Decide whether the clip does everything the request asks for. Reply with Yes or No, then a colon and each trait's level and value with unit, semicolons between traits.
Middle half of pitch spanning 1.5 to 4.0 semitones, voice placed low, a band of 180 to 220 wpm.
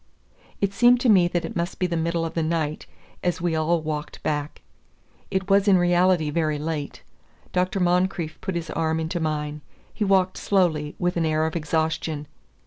No: narrow, 2.6 semitones; medium, 170 Hz; average, 185 wpm